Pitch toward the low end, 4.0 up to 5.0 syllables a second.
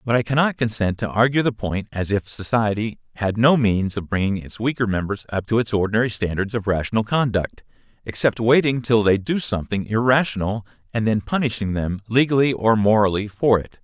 No: low, 110 Hz; 5.6 syllables/s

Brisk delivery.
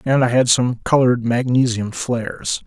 No: average, 160 wpm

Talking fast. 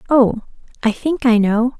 No: average, 165 wpm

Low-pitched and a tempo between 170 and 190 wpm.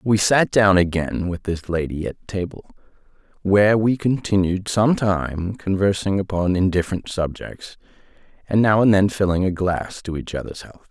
No: very low, 95 Hz; average, 160 wpm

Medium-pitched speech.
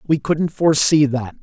Yes: medium, 145 Hz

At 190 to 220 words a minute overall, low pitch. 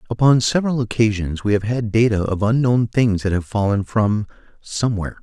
No: average, 160 wpm; low, 110 Hz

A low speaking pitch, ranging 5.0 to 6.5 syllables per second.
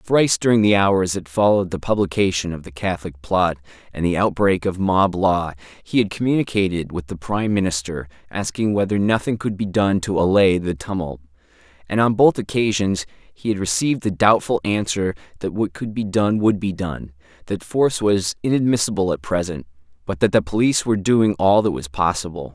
Yes: very low, 95 Hz; 5.4 syllables/s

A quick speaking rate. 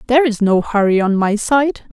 Yes: fast, 210 wpm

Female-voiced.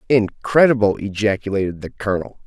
No: male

